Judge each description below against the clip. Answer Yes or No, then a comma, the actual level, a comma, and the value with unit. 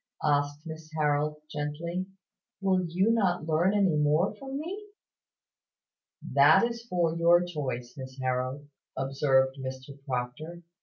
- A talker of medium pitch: Yes, medium, 155 Hz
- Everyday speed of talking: No, slow, 120 wpm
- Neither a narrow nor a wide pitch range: Yes, average, 4.7 semitones